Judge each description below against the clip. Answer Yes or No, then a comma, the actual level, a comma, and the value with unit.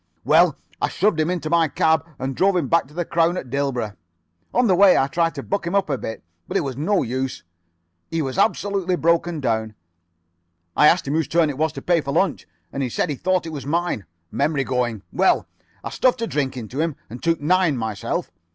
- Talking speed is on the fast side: Yes, fast, 220 wpm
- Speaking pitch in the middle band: Yes, medium, 155 Hz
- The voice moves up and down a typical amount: Yes, average, 4.7 semitones